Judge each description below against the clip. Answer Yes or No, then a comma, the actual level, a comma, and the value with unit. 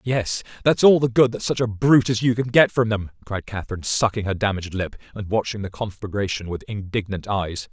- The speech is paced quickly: Yes, fast, 220 wpm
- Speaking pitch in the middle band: No, low, 110 Hz